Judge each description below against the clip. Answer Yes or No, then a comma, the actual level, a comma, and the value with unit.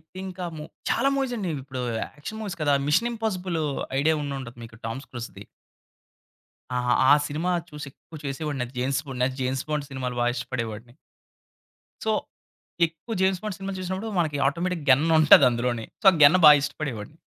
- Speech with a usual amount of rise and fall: No, wide, 6.0 semitones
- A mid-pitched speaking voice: Yes, medium, 150 Hz